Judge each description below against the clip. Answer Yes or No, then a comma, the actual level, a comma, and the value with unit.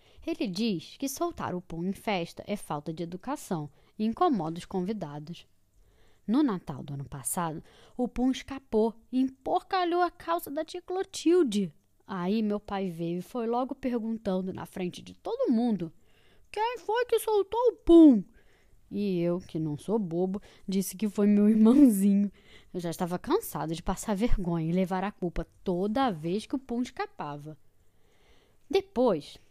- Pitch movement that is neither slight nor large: No, wide, 7.5 semitones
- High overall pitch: Yes, high, 205 Hz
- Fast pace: No, average, 160 wpm